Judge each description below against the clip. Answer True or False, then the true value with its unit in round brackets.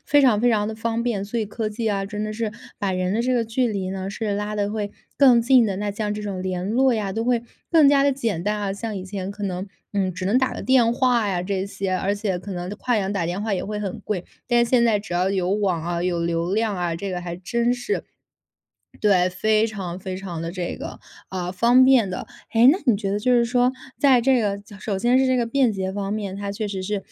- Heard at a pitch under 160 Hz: False (205 Hz)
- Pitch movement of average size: True (3.6 semitones)